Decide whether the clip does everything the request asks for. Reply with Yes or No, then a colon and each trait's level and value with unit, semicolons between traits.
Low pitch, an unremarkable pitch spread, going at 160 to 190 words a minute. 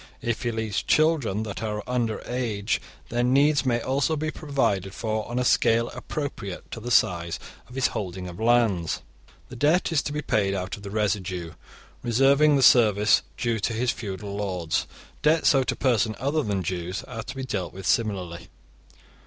Yes: low, 115 Hz; average, 4.8 semitones; average, 180 wpm